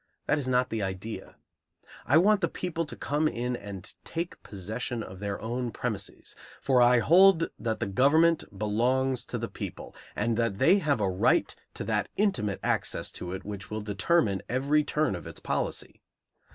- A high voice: No, low, 120 Hz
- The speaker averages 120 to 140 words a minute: No, average, 180 wpm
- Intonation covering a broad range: Yes, wide, 6.7 semitones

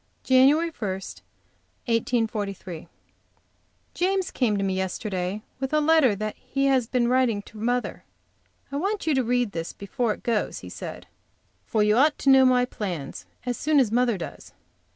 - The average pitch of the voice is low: No, high, 240 Hz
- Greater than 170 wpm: No, average, 160 wpm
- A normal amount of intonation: Yes, average, 4.4 semitones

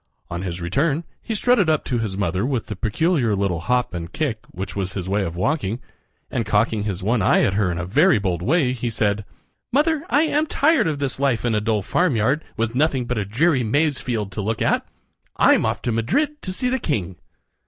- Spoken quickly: Yes, fast, 225 wpm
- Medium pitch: No, low, 115 Hz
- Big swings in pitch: Yes, wide, 7.6 semitones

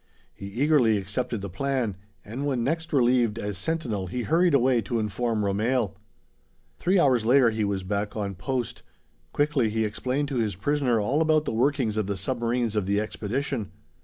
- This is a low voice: Yes, low, 120 Hz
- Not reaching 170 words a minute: No, average, 175 wpm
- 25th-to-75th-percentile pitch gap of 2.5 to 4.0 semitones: No, average, 4.5 semitones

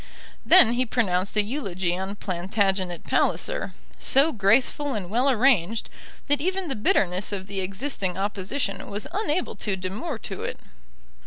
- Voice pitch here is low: No, high, 205 Hz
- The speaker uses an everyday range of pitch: No, wide, 6.0 semitones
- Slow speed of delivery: No, average, 145 wpm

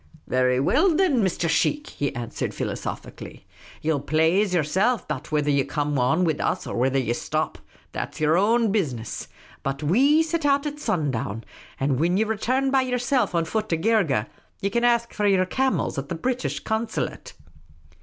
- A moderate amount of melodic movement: No, wide, 8.9 semitones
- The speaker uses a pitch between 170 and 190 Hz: Yes, medium, 185 Hz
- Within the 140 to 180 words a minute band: No, average, 190 wpm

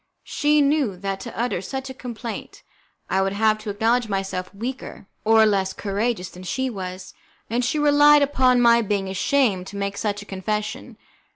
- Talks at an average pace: Yes, average, 175 wpm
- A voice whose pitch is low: No, high, 215 Hz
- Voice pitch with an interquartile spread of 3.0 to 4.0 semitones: No, average, 4.5 semitones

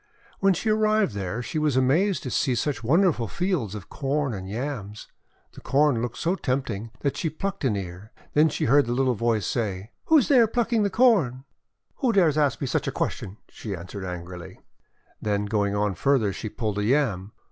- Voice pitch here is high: No, low, 125 Hz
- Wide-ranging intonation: Yes, wide, 7.4 semitones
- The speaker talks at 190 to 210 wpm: Yes, average, 200 wpm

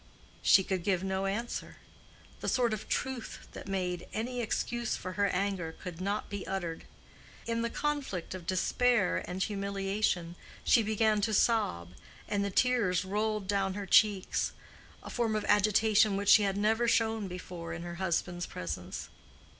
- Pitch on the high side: Yes, high, 200 Hz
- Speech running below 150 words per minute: No, average, 155 wpm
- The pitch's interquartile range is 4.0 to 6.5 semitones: No, average, 3.0 semitones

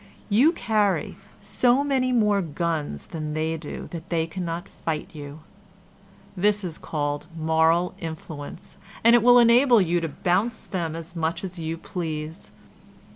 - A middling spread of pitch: Yes, average, 4.5 semitones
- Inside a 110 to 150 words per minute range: Yes, average, 145 wpm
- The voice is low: No, medium, 170 Hz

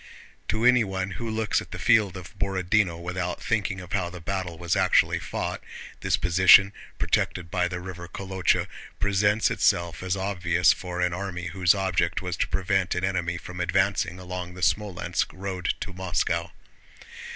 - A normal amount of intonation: No, narrow, 1.9 semitones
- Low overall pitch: Yes, very low, 90 Hz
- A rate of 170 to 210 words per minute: No, average, 160 wpm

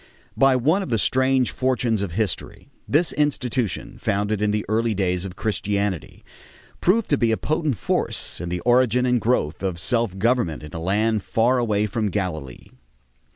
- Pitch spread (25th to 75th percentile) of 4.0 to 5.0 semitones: Yes, average, 4.5 semitones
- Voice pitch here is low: Yes, low, 110 Hz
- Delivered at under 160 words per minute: No, average, 170 wpm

